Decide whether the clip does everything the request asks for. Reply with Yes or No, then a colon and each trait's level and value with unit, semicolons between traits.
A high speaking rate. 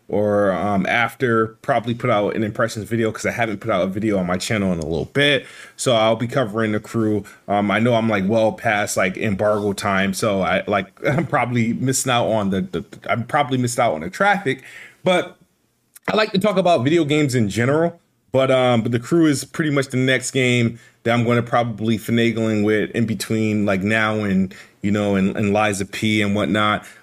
Yes: fast, 215 wpm